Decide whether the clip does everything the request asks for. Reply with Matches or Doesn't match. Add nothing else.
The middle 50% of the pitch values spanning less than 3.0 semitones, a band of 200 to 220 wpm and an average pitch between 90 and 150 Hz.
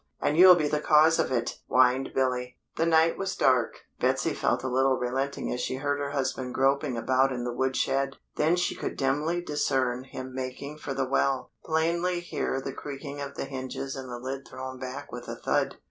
Matches